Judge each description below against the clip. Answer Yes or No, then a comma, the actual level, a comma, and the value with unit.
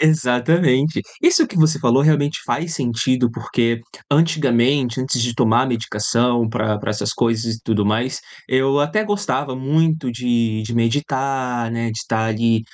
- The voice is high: No, low, 125 Hz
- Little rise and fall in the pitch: No, average, 3.8 semitones